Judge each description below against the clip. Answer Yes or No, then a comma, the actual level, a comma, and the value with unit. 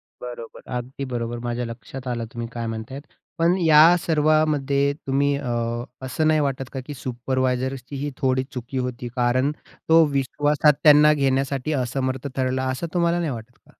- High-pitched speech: No, low, 135 Hz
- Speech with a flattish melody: No, average, 3.0 semitones